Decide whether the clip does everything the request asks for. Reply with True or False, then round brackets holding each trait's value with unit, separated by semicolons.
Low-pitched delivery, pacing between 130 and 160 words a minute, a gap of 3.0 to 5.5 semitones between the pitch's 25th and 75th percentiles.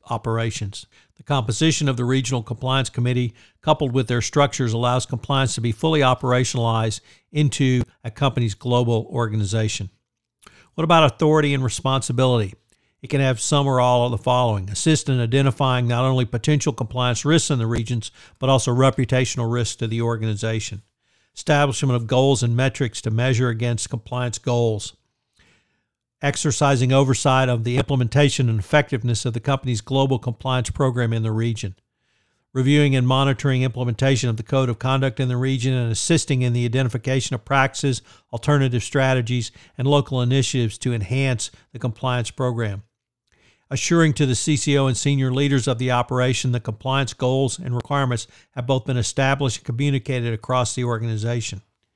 False (125 Hz; 155 wpm; 2.4 semitones)